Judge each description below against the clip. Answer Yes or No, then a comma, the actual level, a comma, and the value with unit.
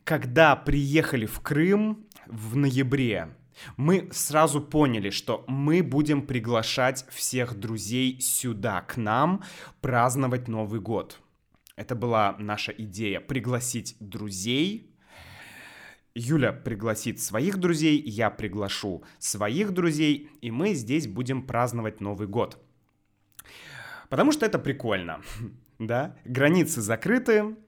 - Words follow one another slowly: Yes, slow, 105 wpm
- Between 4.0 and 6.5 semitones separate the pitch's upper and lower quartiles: Yes, average, 5.2 semitones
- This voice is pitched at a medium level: No, low, 125 Hz